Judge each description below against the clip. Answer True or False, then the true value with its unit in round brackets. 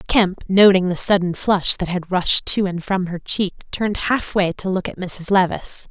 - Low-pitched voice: False (185 Hz)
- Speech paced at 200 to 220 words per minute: True (205 wpm)